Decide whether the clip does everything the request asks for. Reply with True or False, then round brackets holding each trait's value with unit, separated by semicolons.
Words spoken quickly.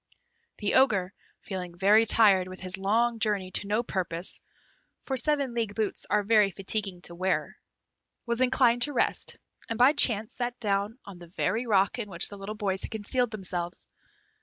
False (180 wpm)